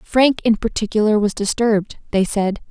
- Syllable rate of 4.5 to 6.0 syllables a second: Yes, 5.0 syllables/s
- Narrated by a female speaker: Yes, female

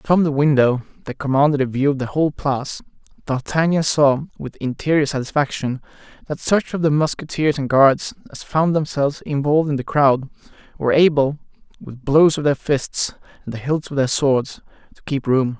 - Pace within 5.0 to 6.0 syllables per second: Yes, 5.2 syllables/s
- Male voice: Yes, male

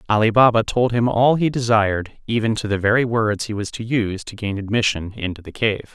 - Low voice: Yes, low, 110 Hz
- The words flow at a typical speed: No, fast, 220 wpm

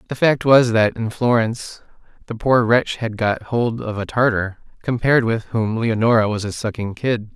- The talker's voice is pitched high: No, low, 115 Hz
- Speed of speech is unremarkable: Yes, average, 190 wpm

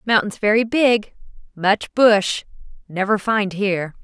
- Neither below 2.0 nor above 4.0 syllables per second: Yes, 3.9 syllables/s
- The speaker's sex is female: Yes, female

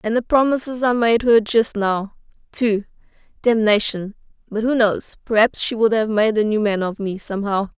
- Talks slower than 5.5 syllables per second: Yes, 5.0 syllables/s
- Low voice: No, high, 220 Hz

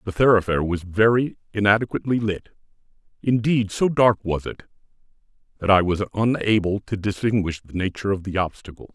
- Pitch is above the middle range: No, low, 100 Hz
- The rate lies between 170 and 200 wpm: No, average, 150 wpm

